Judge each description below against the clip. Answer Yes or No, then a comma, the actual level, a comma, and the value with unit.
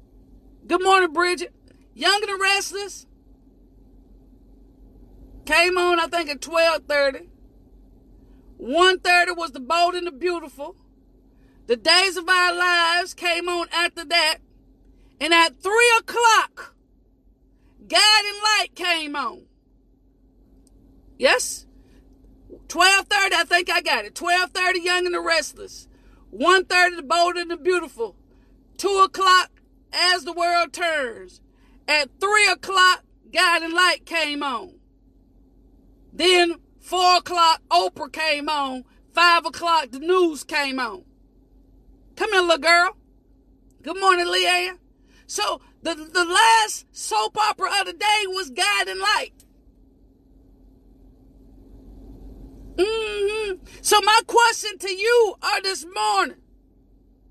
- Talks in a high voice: Yes, very high, 360 Hz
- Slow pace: Yes, slow, 115 wpm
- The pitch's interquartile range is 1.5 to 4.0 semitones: Yes, narrow, 2.5 semitones